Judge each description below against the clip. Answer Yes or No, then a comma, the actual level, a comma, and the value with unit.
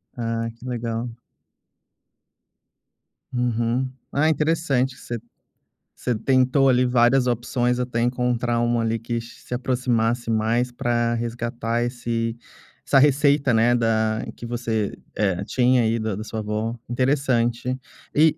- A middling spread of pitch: No, narrow, 1.7 semitones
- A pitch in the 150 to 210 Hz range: No, low, 120 Hz